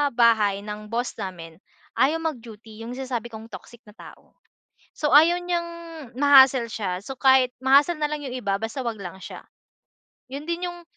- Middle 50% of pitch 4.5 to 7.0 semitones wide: Yes, average, 5.1 semitones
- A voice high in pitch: Yes, high, 245 Hz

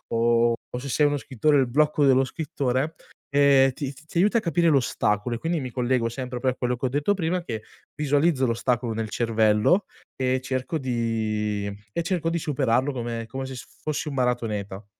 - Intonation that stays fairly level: No, average, 3.9 semitones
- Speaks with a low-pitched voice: Yes, low, 130 Hz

